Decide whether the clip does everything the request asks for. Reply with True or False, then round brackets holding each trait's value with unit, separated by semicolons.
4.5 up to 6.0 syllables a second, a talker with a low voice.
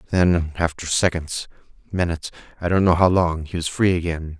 True (5.3 syllables/s; 85 Hz)